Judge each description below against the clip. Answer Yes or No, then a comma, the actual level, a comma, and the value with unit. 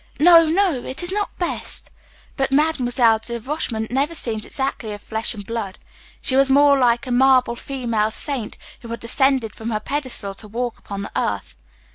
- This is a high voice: Yes, high, 245 Hz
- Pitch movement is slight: No, average, 3.9 semitones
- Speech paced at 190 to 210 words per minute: No, average, 180 wpm